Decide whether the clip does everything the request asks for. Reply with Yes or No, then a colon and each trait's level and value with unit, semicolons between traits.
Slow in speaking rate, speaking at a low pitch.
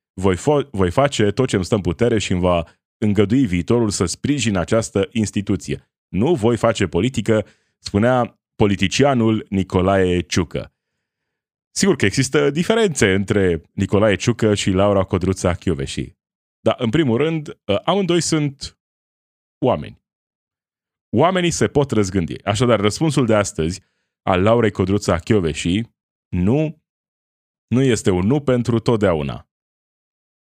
No: average, 125 wpm; low, 105 Hz